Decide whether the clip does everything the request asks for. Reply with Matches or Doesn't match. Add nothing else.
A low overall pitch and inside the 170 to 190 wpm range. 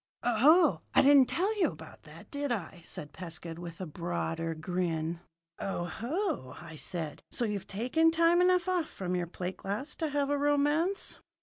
Doesn't match